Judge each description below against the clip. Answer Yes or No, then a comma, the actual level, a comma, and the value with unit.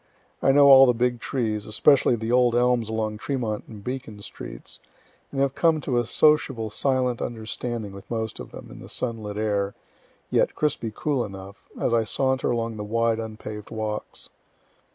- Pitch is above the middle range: No, low, 115 Hz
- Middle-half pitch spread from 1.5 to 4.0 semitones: Yes, average, 2.9 semitones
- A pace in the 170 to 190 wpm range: Yes, average, 175 wpm